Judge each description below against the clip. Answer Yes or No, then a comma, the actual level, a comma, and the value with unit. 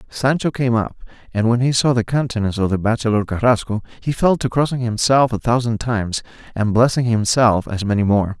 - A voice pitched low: Yes, low, 115 Hz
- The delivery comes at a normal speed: Yes, average, 195 wpm